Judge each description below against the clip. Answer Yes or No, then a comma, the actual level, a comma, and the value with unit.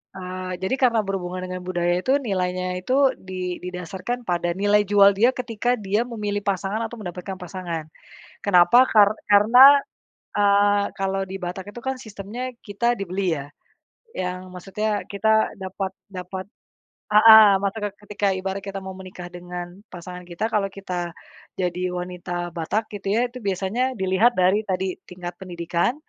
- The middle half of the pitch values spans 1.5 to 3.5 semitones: Yes, average, 2.8 semitones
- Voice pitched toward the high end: Yes, high, 195 Hz